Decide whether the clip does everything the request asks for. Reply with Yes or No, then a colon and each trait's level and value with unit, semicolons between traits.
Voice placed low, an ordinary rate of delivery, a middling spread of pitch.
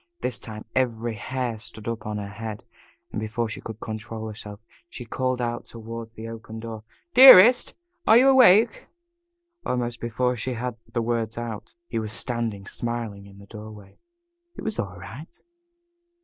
No: low, 115 Hz; average, 165 wpm; narrow, 2.3 semitones